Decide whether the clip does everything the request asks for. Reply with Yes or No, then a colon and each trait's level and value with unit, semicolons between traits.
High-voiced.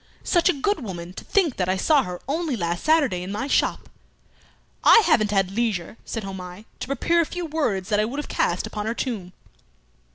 Yes: high, 220 Hz